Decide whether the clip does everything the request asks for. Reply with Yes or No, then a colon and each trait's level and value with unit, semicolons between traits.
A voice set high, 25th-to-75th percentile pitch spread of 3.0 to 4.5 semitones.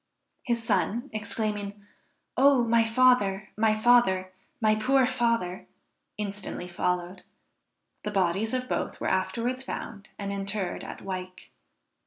Yes: high, 215 Hz; average, 3.5 semitones